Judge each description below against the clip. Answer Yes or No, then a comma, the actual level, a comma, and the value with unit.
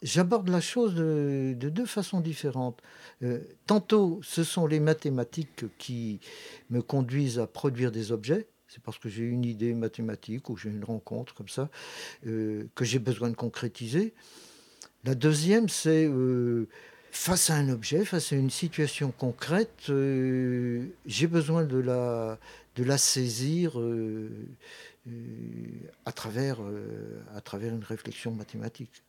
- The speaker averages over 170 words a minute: No, slow, 145 wpm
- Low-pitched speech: Yes, low, 130 Hz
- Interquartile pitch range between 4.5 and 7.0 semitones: Yes, average, 5.2 semitones